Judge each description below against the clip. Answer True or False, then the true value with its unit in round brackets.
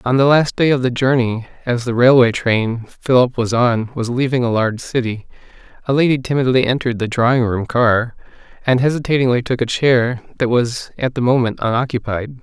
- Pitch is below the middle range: True (125 Hz)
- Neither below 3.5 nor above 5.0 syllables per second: False (5.4 syllables/s)